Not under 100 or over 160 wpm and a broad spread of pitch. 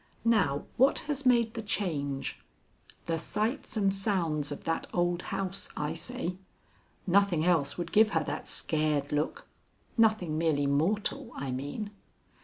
Yes: average, 140 wpm; wide, 5.9 semitones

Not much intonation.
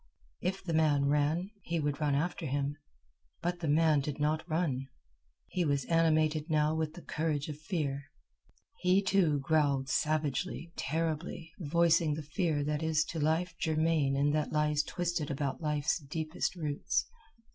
Yes: narrow, 2.1 semitones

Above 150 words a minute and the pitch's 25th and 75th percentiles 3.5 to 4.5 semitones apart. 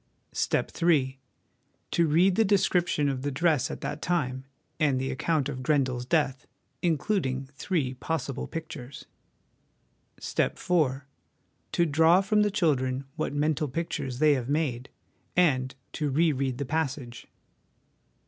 No: average, 145 wpm; average, 4.1 semitones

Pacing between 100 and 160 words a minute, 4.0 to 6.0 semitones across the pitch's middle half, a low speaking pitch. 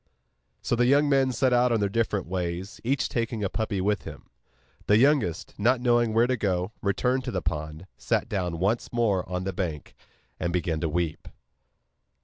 No: average, 185 wpm; average, 5.2 semitones; low, 105 Hz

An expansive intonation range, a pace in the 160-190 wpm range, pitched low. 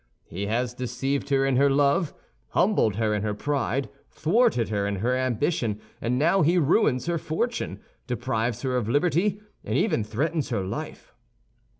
Yes: wide, 5.7 semitones; average, 165 wpm; low, 130 Hz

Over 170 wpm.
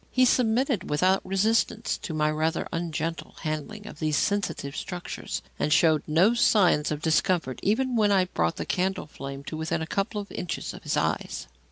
Yes: average, 180 wpm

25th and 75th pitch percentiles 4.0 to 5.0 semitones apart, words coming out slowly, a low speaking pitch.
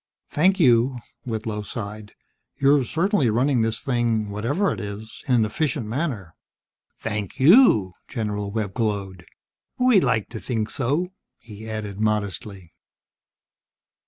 Yes: average, 4.3 semitones; slow, 125 wpm; low, 110 Hz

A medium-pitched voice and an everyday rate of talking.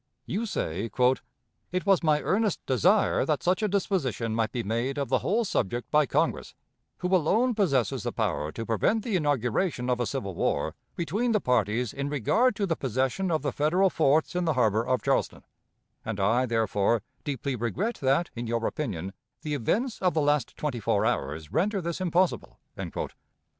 Yes: medium, 145 Hz; average, 180 wpm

